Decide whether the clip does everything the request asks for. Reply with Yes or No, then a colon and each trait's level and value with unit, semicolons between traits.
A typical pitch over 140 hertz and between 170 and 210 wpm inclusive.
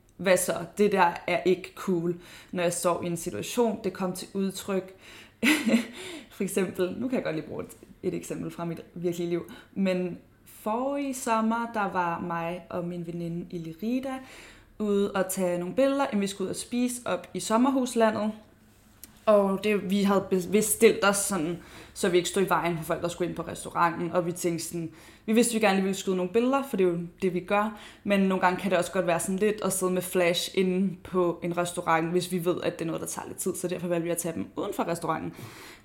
No: medium, 185 Hz; fast, 225 wpm